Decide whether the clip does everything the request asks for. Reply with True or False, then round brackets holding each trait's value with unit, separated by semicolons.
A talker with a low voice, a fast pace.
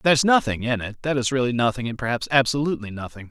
True (125 Hz; 220 wpm)